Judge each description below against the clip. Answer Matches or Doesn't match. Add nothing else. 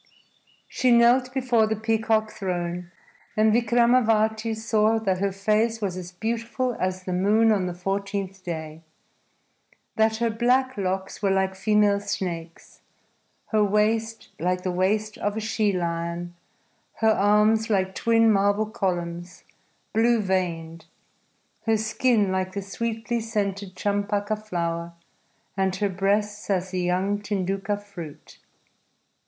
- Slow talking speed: Matches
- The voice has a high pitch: Matches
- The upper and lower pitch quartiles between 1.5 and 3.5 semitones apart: Matches